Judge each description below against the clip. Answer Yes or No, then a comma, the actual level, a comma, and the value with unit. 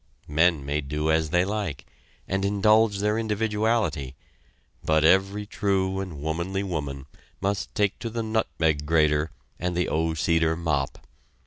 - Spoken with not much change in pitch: No, average, 4.7 semitones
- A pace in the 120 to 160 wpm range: Yes, average, 140 wpm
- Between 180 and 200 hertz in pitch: No, very low, 90 Hz